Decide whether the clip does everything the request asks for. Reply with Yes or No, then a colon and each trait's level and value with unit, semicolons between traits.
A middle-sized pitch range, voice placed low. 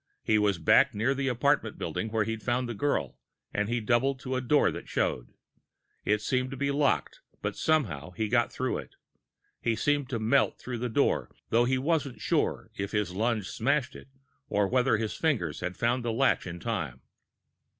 Yes: average, 3.9 semitones; low, 120 Hz